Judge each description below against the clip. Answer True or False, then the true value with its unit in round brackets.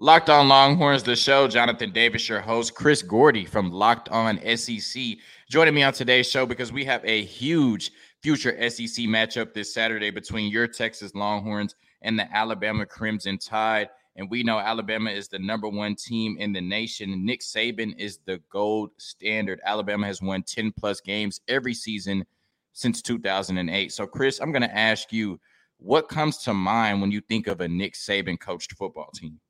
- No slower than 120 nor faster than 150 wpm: False (180 wpm)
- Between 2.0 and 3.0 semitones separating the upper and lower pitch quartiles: True (2.5 semitones)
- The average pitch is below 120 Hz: True (110 Hz)